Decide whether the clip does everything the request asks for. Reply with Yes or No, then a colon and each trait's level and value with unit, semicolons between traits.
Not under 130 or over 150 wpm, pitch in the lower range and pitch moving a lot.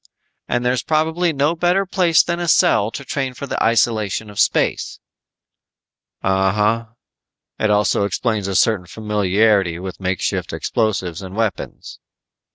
Yes: average, 140 wpm; low, 110 Hz; wide, 6.1 semitones